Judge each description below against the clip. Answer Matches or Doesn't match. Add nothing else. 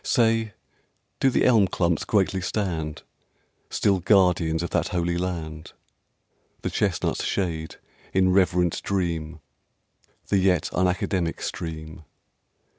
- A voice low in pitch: Matches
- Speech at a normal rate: Doesn't match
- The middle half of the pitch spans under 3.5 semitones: Matches